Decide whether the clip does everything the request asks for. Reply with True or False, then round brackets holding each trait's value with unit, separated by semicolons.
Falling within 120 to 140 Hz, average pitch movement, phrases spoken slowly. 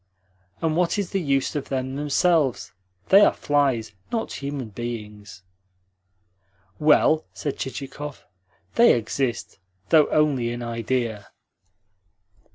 True (135 Hz; 4.4 semitones; 110 wpm)